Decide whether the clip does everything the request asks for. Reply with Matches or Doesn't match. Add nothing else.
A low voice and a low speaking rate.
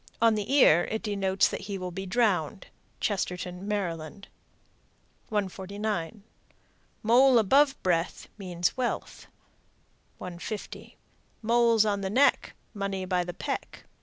Doesn't match